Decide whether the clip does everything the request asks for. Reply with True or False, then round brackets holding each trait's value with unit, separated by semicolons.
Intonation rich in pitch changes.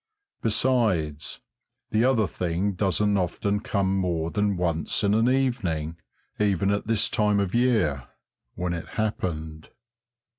False (4.2 semitones)